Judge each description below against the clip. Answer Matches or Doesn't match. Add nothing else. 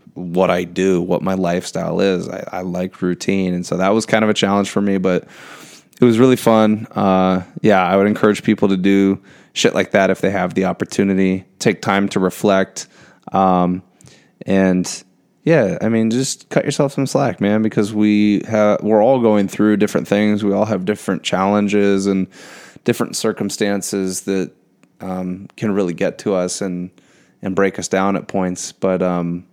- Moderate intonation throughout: Doesn't match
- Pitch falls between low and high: Doesn't match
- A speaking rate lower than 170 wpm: Doesn't match